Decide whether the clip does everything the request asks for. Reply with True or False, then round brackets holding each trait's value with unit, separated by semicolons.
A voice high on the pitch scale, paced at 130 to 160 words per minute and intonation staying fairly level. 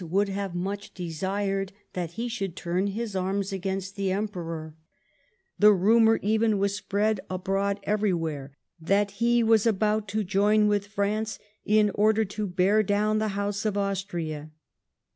True (200 Hz; 145 wpm; 2.0 semitones)